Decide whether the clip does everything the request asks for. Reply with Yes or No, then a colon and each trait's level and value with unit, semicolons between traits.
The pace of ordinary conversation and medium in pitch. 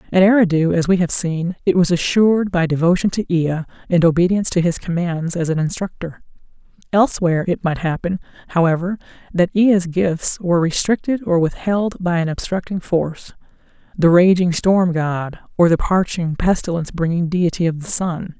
Yes: average, 160 wpm; medium, 175 Hz